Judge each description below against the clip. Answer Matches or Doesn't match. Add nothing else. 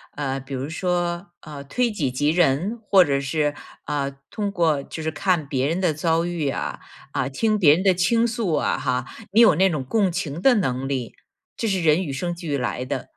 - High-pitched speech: Doesn't match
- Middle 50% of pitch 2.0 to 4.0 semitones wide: Doesn't match